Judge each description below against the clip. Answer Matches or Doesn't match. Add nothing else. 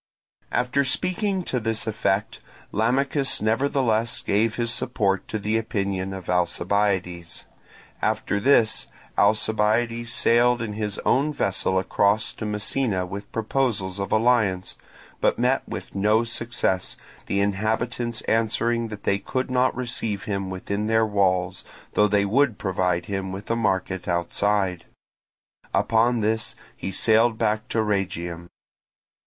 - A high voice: Doesn't match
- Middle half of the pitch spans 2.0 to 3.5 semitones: Matches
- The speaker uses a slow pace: Matches